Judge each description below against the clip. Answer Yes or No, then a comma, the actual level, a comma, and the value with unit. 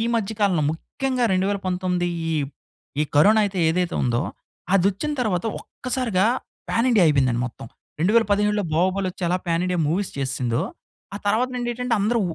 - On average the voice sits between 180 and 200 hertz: Yes, high, 190 Hz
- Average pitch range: Yes, average, 4.2 semitones